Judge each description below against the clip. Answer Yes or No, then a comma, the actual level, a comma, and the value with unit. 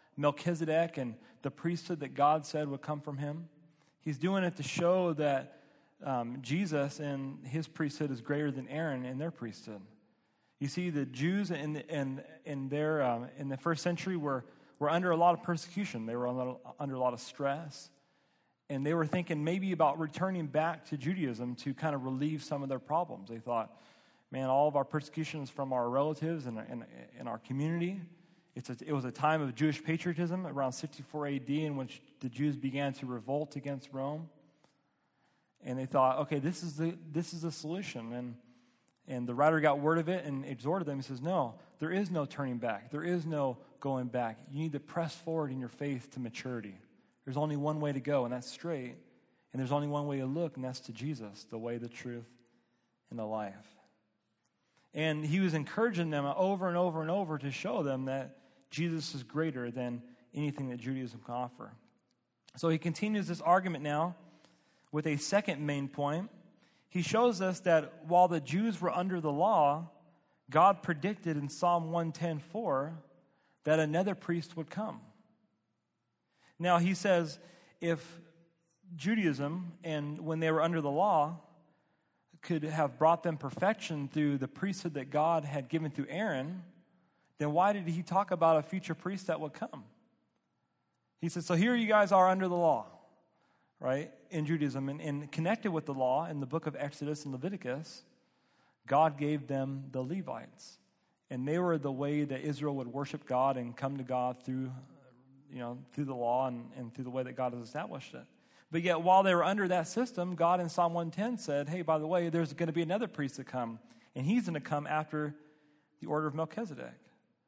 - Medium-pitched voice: Yes, medium, 150 Hz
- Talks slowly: No, average, 190 wpm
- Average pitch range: Yes, average, 3.9 semitones